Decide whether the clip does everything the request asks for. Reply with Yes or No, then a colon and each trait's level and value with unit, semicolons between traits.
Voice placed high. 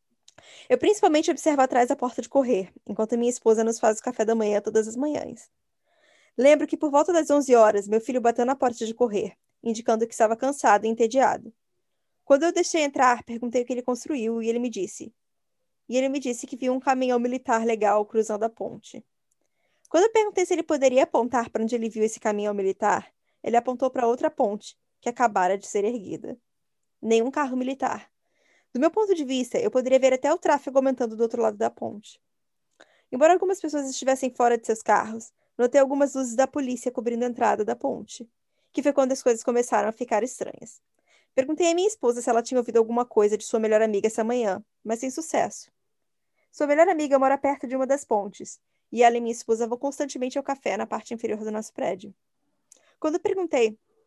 Yes: very high, 250 Hz